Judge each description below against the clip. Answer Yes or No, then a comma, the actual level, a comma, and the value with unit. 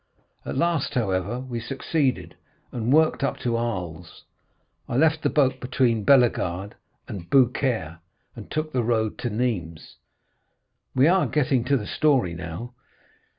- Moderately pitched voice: No, low, 120 Hz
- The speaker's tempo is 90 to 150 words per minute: Yes, average, 140 wpm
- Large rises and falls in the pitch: No, average, 5.0 semitones